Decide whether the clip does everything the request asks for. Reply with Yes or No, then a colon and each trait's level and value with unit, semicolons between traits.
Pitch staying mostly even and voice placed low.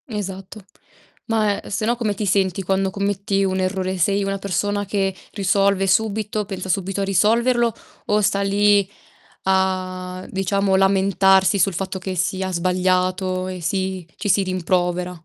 No: narrow, 1.4 semitones; high, 195 Hz